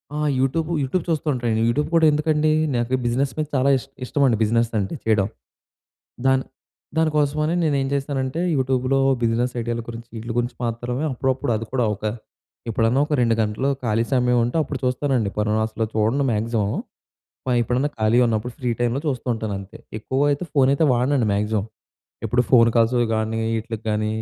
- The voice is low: Yes, low, 120 Hz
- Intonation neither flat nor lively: Yes, average, 3.2 semitones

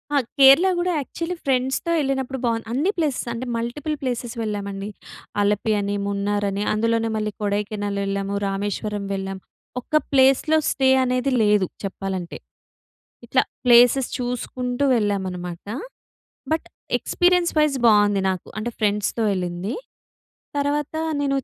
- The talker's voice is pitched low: No, high, 230 Hz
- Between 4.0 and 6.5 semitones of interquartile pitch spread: Yes, average, 4.9 semitones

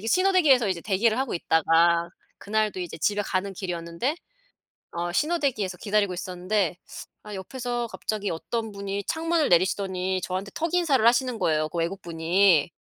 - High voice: Yes, high, 200 Hz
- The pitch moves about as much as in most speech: Yes, average, 5.0 semitones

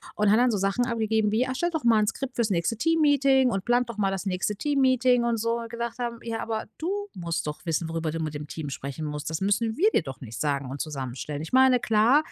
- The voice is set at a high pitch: Yes, high, 220 Hz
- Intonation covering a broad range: Yes, wide, 7.0 semitones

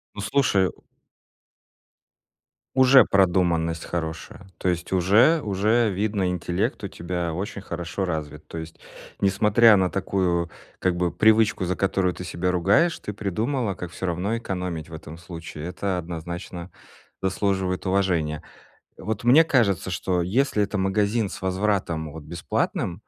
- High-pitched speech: No, very low, 95 Hz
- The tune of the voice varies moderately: Yes, average, 3.1 semitones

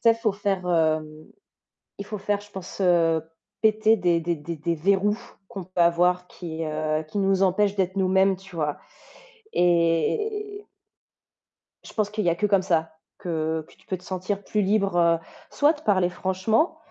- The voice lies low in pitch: No, medium, 185 Hz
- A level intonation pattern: No, average, 3.4 semitones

